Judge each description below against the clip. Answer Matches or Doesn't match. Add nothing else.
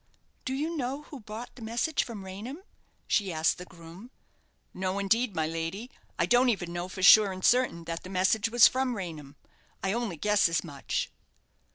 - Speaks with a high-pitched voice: Matches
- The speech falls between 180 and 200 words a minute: Matches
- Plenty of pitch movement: Matches